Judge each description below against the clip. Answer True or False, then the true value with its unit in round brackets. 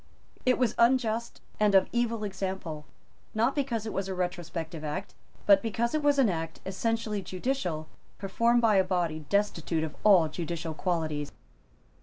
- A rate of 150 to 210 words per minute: True (155 wpm)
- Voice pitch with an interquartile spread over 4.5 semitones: True (5.3 semitones)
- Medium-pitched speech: False (195 Hz)